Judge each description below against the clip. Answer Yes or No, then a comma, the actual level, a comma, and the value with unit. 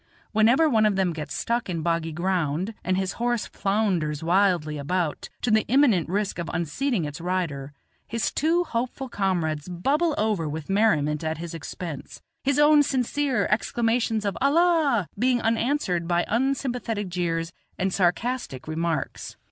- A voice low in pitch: No, high, 195 Hz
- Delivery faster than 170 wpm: No, average, 150 wpm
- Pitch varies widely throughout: Yes, wide, 6.4 semitones